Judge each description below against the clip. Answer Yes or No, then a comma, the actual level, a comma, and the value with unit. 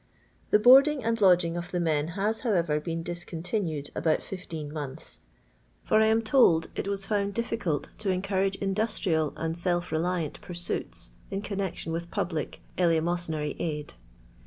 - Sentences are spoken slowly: No, average, 150 wpm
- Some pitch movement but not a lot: Yes, average, 3.7 semitones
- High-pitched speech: No, medium, 175 Hz